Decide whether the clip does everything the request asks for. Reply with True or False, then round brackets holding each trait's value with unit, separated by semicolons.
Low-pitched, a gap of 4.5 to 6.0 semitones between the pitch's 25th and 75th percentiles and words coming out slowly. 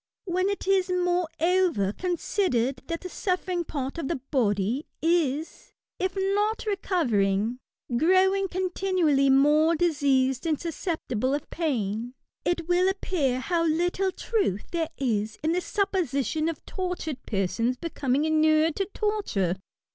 False (325 Hz; 5.7 semitones; 125 wpm)